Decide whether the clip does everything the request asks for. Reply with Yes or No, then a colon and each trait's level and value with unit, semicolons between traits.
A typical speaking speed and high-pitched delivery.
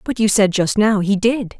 No: fast, 265 wpm; high, 205 Hz